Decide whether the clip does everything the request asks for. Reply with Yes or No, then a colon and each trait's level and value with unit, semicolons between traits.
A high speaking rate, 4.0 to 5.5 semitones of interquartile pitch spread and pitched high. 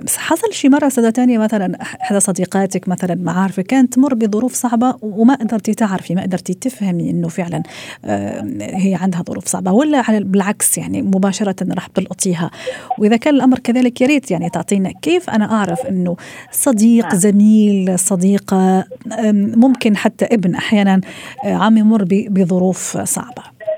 Yes: fast, 150 wpm; average, 4.3 semitones; high, 210 Hz